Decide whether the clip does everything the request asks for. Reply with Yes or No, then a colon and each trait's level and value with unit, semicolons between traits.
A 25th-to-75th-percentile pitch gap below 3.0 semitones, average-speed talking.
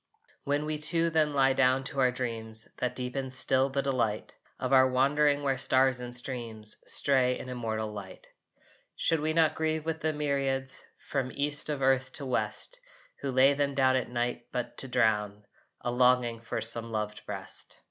Yes: narrow, 2.6 semitones; average, 180 wpm